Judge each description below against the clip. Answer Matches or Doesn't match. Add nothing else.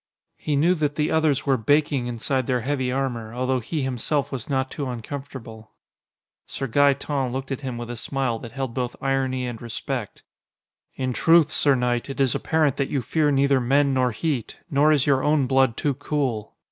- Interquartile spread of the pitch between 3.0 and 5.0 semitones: Doesn't match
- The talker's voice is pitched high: Doesn't match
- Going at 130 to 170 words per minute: Doesn't match